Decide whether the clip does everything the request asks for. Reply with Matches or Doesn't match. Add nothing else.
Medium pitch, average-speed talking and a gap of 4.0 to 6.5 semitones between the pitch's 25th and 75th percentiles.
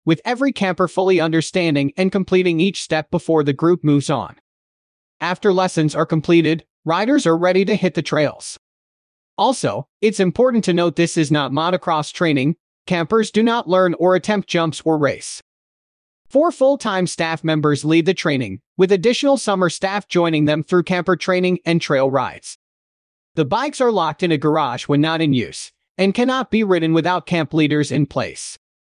Doesn't match